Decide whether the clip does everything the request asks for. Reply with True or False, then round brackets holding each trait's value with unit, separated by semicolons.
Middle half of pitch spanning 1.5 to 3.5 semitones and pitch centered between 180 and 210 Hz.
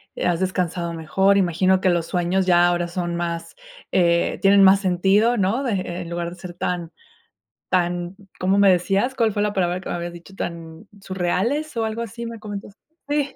True (2.5 semitones; 185 Hz)